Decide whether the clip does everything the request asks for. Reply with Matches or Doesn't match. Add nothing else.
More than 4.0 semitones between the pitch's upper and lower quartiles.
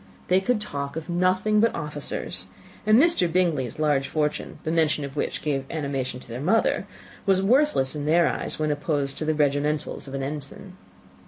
Matches